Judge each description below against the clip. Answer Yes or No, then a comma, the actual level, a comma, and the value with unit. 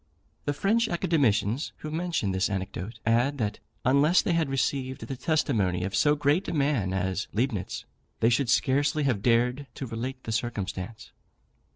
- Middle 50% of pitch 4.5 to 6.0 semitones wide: Yes, wide, 5.5 semitones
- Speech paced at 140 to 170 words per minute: Yes, average, 160 wpm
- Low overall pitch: Yes, low, 130 Hz